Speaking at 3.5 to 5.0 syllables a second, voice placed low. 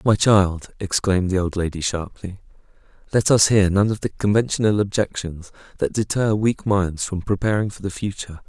No: 5.2 syllables/s; low, 100 Hz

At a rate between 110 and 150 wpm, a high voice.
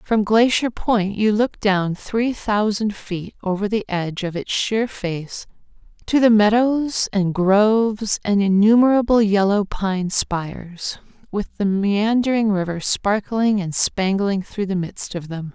Yes: average, 145 wpm; high, 205 Hz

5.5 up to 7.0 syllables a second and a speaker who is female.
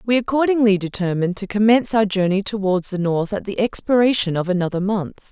Yes: 6.0 syllables/s; female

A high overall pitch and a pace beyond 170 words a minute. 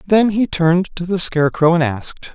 No: medium, 170 Hz; fast, 205 wpm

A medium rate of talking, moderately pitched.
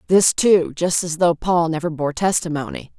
Yes: average, 180 wpm; medium, 170 Hz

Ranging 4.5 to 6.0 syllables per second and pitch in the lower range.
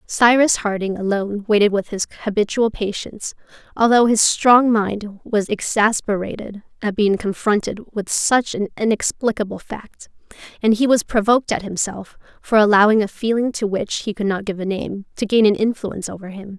No: 5.1 syllables/s; high, 210 Hz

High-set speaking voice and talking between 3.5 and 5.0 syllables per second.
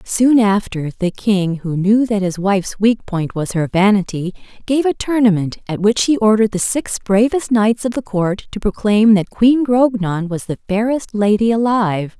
Yes: high, 210 Hz; 4.6 syllables/s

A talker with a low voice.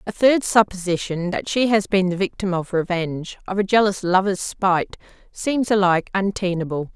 No: high, 190 Hz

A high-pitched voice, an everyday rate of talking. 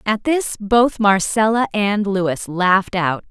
Yes: high, 205 Hz; average, 145 wpm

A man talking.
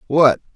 Yes: male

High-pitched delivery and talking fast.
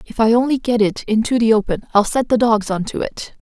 Yes: high, 225 Hz; fast, 260 wpm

